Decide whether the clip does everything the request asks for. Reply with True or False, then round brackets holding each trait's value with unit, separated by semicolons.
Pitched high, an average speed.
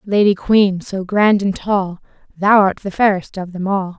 True (195 Hz; 195 wpm)